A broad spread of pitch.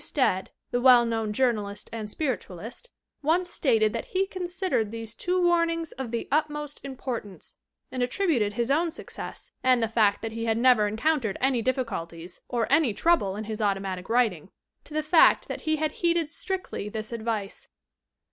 Yes: wide, 6.2 semitones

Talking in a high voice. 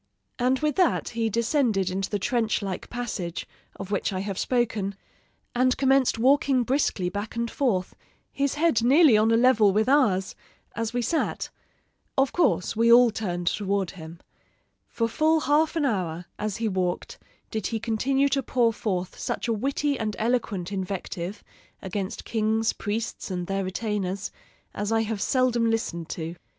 Yes: high, 225 Hz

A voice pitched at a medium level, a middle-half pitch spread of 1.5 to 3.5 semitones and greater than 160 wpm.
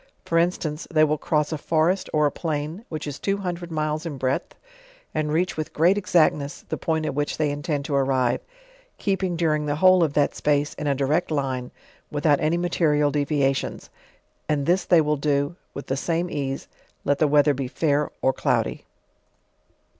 Yes: medium, 150 Hz; narrow, 2.6 semitones; average, 185 wpm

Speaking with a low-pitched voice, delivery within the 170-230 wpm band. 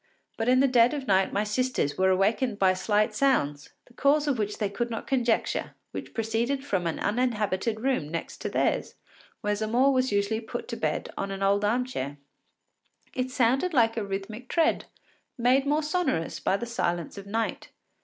No: high, 225 Hz; average, 185 wpm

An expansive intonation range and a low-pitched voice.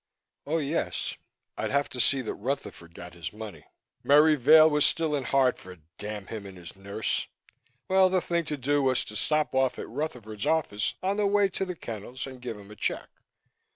Yes: wide, 6.8 semitones; low, 130 Hz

